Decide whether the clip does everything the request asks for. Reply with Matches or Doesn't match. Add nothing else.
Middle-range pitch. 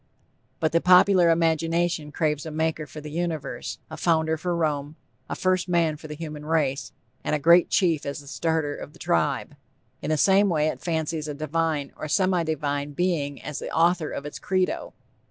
Matches